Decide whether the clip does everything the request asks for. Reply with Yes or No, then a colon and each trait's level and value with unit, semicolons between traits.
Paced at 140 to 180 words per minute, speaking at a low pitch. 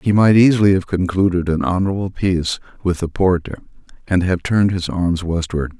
Yes: average, 175 wpm; very low, 90 Hz